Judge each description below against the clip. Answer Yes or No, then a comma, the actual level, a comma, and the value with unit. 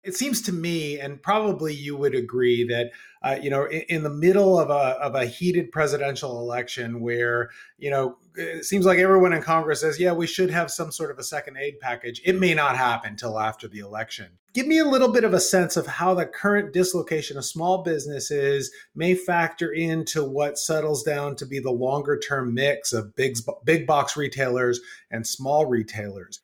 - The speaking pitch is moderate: Yes, medium, 145 Hz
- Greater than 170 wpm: Yes, average, 200 wpm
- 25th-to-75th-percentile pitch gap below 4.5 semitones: No, average, 5.1 semitones